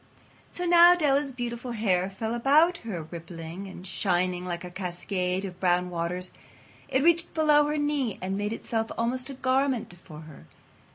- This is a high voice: Yes, high, 210 Hz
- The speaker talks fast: No, average, 165 wpm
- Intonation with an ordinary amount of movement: No, wide, 7.2 semitones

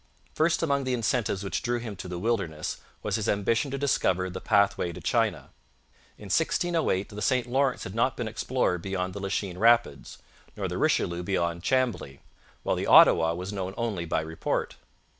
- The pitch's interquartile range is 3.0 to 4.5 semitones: No, average, 5.1 semitones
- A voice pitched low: Yes, low, 100 Hz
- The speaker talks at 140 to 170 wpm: No, average, 180 wpm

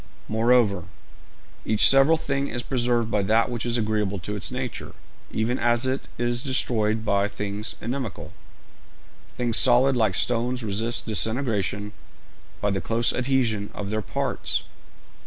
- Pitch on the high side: No, low, 115 Hz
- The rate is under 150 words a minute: Yes, average, 140 wpm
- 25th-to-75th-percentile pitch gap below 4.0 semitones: Yes, average, 3.0 semitones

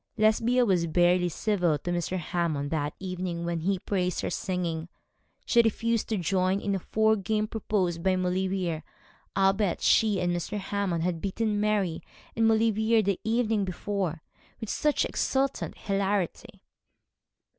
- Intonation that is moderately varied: Yes, average, 3.5 semitones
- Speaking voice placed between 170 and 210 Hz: Yes, high, 190 Hz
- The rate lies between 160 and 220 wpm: No, average, 145 wpm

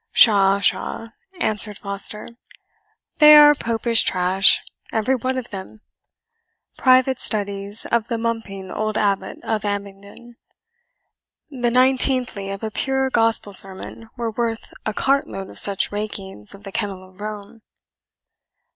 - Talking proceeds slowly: Yes, slow, 130 wpm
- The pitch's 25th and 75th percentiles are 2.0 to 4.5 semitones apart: Yes, average, 3.1 semitones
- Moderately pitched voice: No, high, 215 Hz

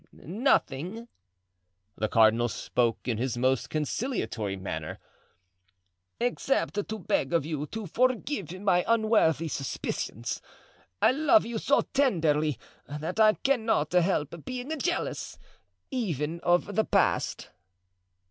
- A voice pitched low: No, medium, 160 Hz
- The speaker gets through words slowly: Yes, slow, 105 wpm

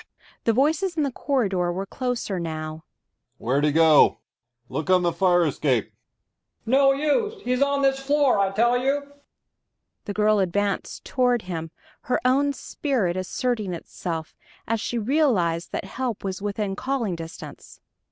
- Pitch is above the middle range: Yes, high, 215 Hz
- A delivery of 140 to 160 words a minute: Yes, average, 150 wpm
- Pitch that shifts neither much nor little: No, wide, 7.3 semitones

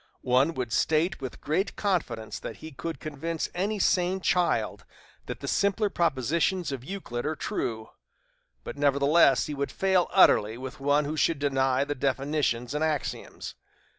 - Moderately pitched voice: Yes, medium, 150 Hz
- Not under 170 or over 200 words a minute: No, average, 155 wpm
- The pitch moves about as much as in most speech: Yes, average, 4.3 semitones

